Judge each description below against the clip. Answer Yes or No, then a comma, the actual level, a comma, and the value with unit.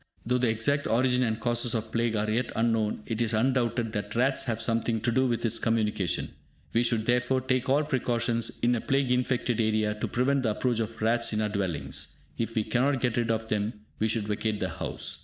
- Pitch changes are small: Yes, narrow, 2.1 semitones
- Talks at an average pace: No, fast, 215 wpm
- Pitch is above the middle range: No, low, 115 Hz